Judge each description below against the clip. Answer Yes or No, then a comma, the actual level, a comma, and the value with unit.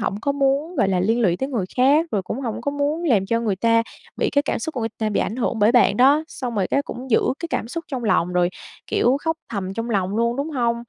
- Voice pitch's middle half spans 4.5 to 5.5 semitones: Yes, average, 5.0 semitones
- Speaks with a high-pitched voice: Yes, high, 235 Hz